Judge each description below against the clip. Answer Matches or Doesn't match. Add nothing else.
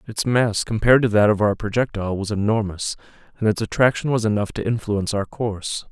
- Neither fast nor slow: Matches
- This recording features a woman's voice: Doesn't match